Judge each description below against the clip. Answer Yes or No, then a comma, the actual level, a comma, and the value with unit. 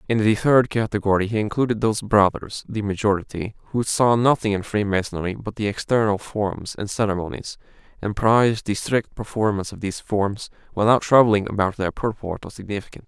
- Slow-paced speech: No, average, 165 wpm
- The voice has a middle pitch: No, low, 105 Hz